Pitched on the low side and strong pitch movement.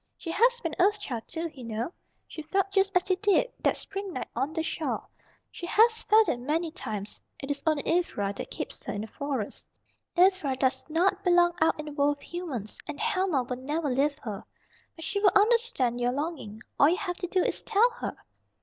No: very high, 325 Hz; wide, 6.3 semitones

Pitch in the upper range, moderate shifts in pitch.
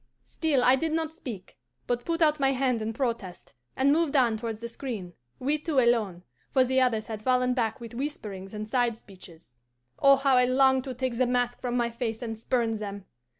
Yes: high, 245 Hz; average, 3.1 semitones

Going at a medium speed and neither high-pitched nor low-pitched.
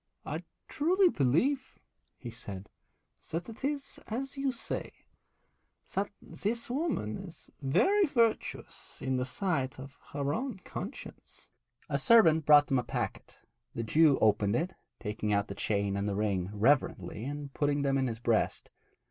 Yes: average, 150 wpm; medium, 145 Hz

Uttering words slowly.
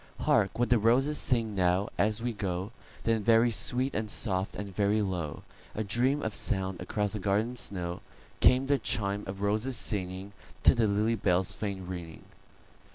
No: average, 155 wpm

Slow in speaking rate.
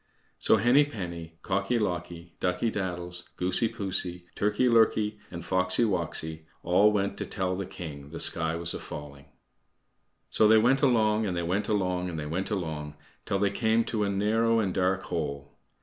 No: average, 175 wpm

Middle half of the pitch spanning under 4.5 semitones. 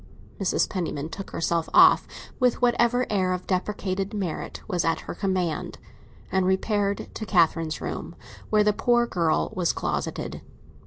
Yes: average, 3.4 semitones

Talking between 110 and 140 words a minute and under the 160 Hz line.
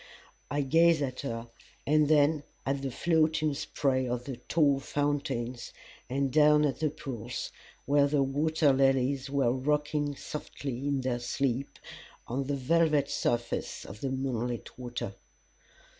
Yes: slow, 135 wpm; medium, 140 Hz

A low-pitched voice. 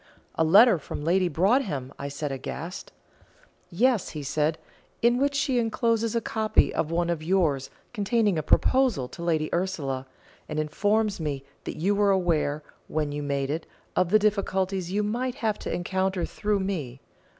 No: medium, 185 Hz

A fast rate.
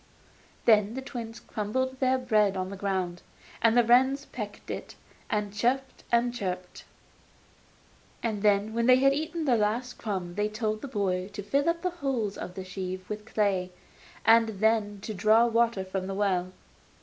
No: average, 170 wpm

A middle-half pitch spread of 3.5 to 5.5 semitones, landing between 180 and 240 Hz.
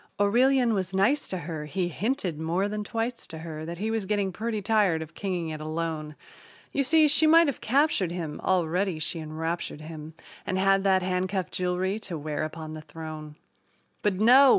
Yes: average, 4.8 semitones; medium, 185 Hz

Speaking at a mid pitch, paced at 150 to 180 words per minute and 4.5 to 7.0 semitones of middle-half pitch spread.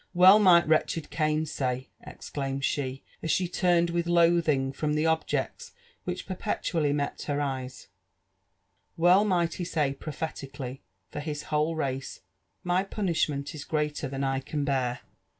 No: medium, 150 Hz; average, 160 wpm; average, 3.7 semitones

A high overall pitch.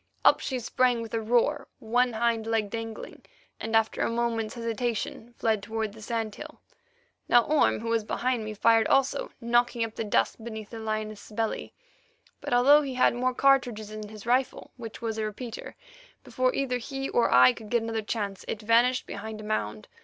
Yes: high, 230 Hz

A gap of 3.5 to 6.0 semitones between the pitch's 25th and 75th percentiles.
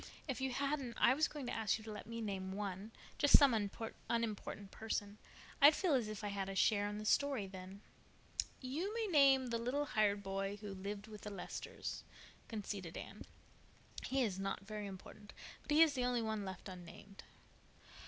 Yes: average, 4.5 semitones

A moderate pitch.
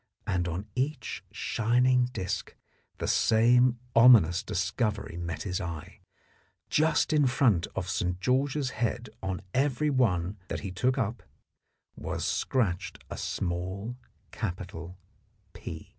No: low, 105 Hz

